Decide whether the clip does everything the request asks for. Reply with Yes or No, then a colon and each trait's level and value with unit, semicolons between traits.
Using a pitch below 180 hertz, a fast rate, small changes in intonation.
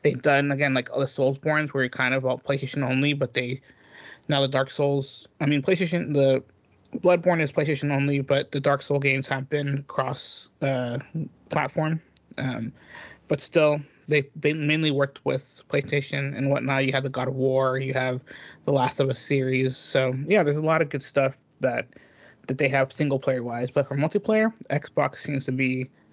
No: medium, 140 Hz; average, 190 wpm; narrow, 1.8 semitones